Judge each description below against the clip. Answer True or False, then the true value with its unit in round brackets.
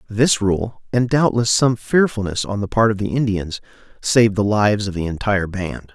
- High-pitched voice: False (105 Hz)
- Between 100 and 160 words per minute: False (190 wpm)